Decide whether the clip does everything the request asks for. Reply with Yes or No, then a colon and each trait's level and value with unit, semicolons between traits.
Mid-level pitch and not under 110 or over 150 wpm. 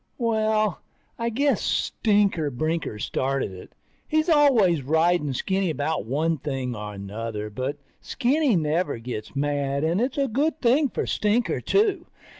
Yes: medium, 165 Hz; average, 140 wpm